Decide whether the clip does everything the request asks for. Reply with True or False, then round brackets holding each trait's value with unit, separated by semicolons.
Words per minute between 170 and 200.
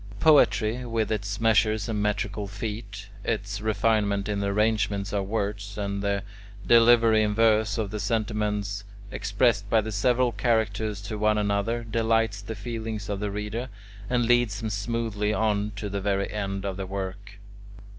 False (160 wpm)